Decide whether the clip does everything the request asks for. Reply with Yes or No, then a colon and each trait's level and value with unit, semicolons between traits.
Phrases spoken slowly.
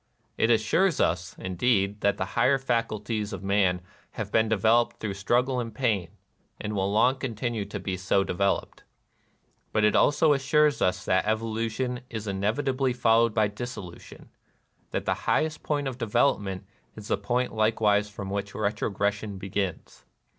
No: average, 160 wpm